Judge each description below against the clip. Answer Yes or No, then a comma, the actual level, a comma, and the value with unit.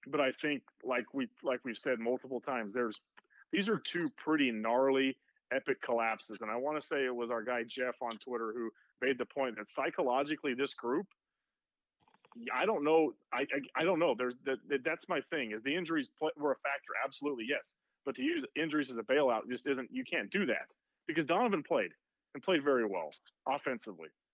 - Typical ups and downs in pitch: Yes, average, 4.2 semitones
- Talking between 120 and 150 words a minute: No, average, 200 wpm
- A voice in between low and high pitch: No, low, 130 Hz